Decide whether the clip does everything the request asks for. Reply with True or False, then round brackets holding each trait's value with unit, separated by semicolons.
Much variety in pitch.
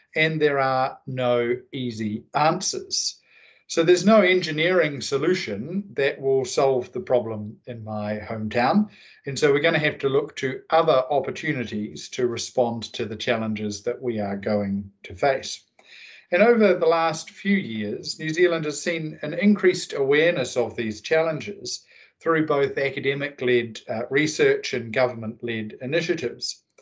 True (7.0 semitones)